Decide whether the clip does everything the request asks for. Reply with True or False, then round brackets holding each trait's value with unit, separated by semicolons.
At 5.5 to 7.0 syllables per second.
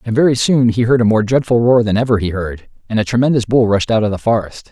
True (6.3 syllables/s)